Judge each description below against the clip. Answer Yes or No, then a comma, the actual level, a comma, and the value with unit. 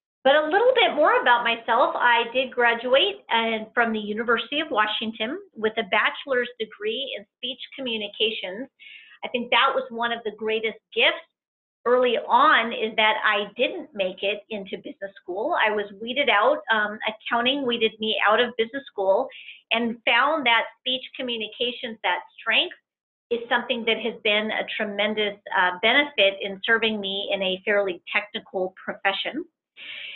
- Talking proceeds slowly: No, average, 155 wpm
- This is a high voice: Yes, high, 230 Hz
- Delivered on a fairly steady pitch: No, average, 3.6 semitones